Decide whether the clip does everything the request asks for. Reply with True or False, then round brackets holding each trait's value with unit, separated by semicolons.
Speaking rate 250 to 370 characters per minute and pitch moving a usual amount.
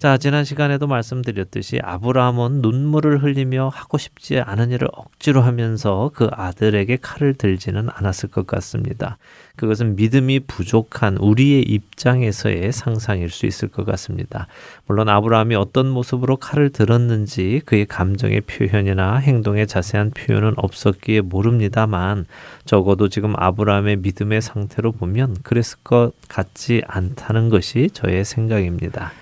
True (340 characters per minute; 3.8 semitones)